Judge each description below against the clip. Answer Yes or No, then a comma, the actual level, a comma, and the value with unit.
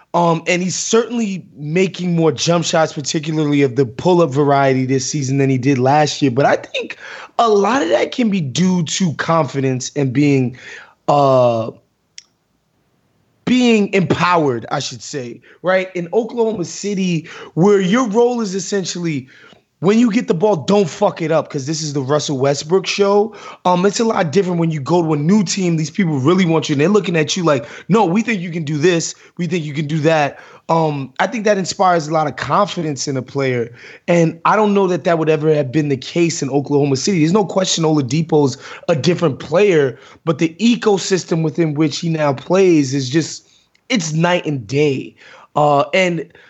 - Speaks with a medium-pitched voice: Yes, medium, 165 Hz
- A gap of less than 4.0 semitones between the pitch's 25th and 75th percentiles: No, average, 4.5 semitones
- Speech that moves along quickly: No, average, 195 wpm